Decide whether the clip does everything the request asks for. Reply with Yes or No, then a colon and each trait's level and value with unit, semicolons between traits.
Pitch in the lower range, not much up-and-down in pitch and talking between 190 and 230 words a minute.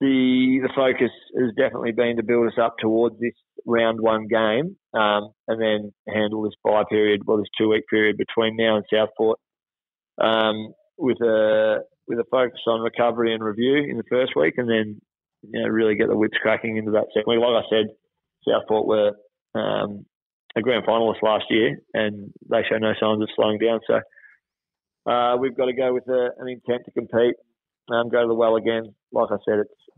Yes: low, 115 Hz; narrow, 1.9 semitones; average, 200 wpm